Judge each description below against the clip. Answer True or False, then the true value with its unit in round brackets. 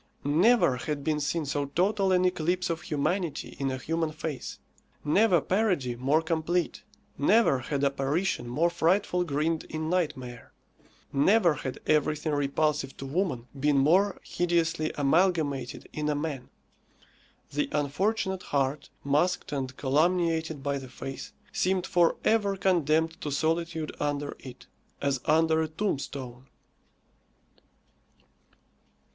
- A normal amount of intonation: True (3.9 semitones)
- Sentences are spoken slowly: True (125 wpm)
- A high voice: False (155 Hz)